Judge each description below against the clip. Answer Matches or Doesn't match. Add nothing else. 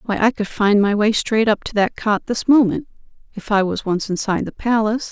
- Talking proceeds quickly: Matches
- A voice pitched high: Matches